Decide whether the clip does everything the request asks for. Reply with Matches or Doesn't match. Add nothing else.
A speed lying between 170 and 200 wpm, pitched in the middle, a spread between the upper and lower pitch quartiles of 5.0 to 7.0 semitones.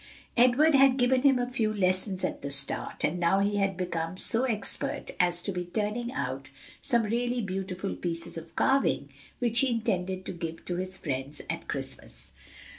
Doesn't match